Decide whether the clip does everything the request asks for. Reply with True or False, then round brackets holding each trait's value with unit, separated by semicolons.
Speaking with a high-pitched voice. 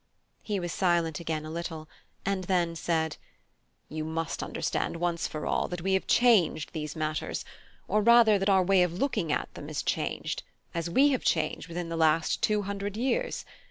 False (175 Hz)